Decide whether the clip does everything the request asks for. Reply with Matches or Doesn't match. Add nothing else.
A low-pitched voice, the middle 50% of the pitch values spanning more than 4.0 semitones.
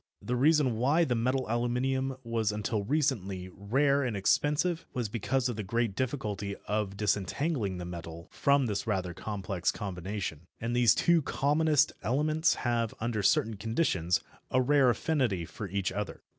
Matches